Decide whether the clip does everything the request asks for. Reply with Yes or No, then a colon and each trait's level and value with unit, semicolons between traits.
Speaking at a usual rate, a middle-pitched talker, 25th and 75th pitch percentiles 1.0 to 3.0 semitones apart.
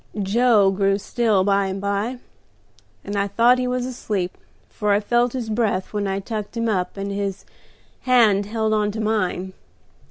No: average, 170 wpm; high, 205 Hz; average, 2.7 semitones